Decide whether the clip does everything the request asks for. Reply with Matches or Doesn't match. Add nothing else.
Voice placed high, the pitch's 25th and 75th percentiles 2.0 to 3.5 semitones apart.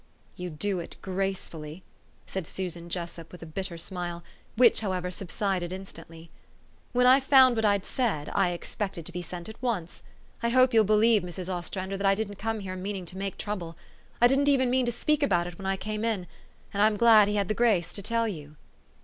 Doesn't match